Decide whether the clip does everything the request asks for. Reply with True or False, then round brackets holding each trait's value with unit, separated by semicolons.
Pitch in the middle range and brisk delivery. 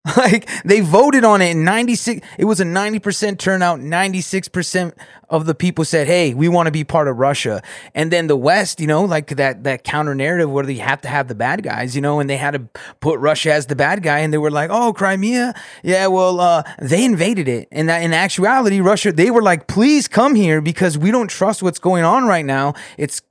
True (175 Hz; 230 wpm)